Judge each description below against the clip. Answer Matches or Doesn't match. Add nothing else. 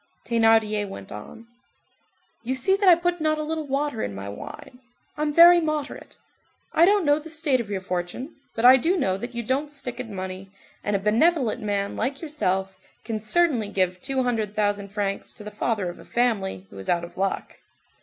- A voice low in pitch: Doesn't match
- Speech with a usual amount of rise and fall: Doesn't match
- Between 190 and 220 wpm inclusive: Matches